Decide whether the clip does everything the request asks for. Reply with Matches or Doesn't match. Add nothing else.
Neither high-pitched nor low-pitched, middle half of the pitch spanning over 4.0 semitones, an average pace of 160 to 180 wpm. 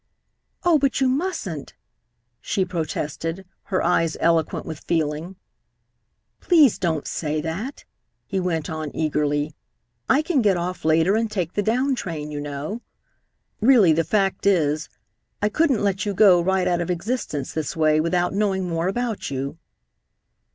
Doesn't match